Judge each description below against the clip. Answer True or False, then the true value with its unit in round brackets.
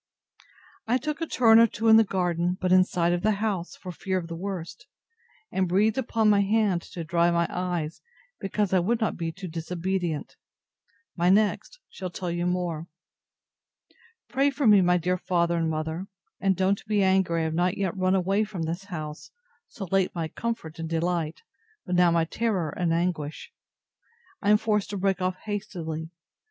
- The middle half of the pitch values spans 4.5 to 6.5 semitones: False (3.2 semitones)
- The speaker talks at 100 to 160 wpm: False (185 wpm)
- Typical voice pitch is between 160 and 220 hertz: True (185 Hz)